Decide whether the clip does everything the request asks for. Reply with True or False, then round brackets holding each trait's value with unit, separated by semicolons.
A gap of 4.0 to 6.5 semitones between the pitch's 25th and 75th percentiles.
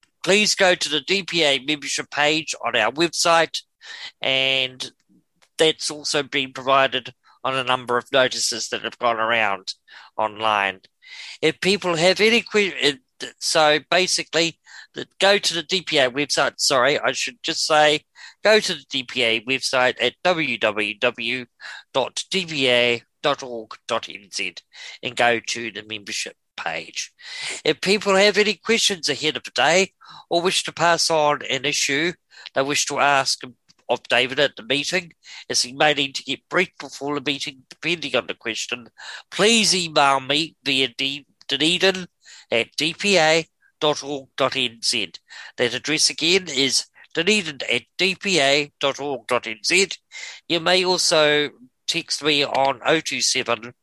True (4.7 semitones)